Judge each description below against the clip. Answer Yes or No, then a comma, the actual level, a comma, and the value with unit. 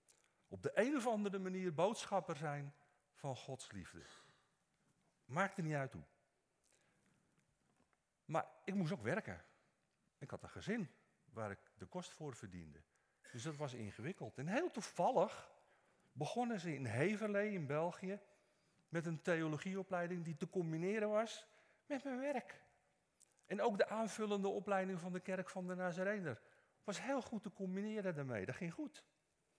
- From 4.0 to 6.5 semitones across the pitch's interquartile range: Yes, average, 5.2 semitones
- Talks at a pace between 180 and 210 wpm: No, average, 150 wpm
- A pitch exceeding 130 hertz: Yes, medium, 185 Hz